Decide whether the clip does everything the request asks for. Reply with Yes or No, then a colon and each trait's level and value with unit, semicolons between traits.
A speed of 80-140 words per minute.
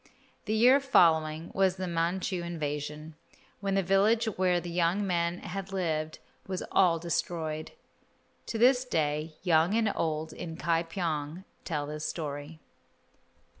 Yes: slow, 135 wpm